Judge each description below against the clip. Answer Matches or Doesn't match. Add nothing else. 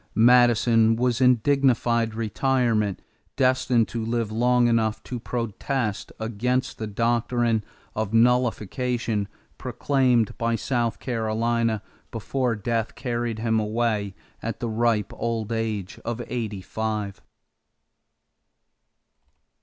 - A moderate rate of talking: Doesn't match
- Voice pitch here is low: Matches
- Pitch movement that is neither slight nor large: Doesn't match